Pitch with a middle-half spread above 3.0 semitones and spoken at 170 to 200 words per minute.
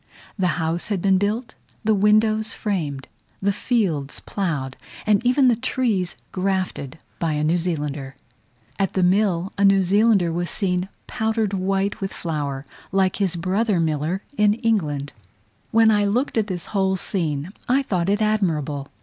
No: average, 4.2 semitones; average, 155 wpm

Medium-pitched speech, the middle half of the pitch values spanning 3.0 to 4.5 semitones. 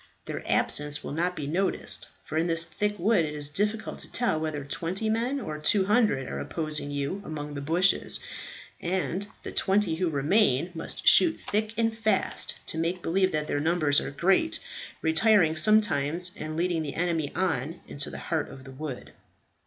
No: medium, 170 Hz; average, 5.1 semitones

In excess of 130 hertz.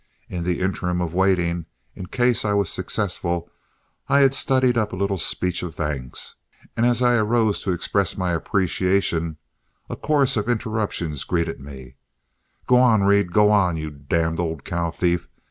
No: very low, 90 Hz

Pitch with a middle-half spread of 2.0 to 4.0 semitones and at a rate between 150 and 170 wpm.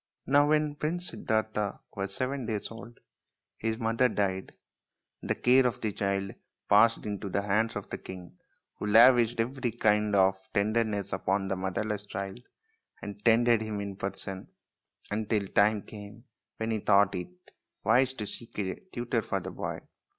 Yes: average, 2.9 semitones; average, 165 wpm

